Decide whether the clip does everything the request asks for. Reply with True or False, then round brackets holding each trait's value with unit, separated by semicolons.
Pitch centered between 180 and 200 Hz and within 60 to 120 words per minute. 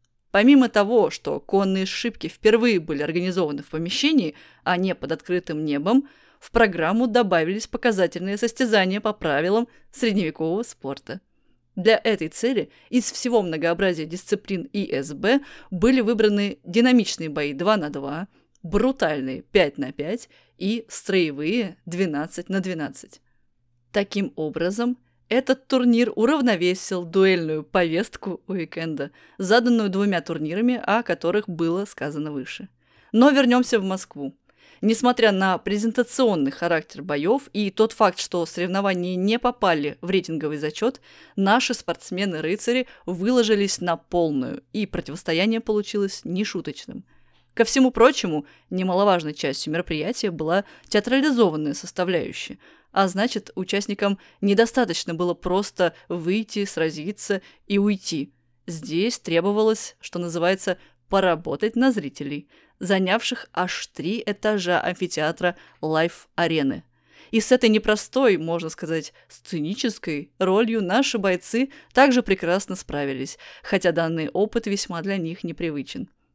True (190 Hz; 115 wpm)